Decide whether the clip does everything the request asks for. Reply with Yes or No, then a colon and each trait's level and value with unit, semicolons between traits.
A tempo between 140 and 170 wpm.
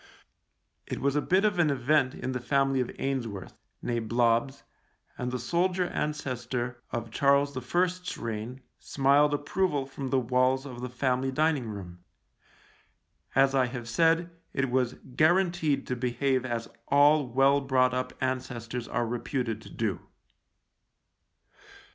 Yes: average, 145 wpm